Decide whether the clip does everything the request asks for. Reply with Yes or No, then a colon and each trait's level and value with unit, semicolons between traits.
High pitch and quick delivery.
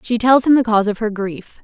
Yes: high, 225 Hz; fast, 295 wpm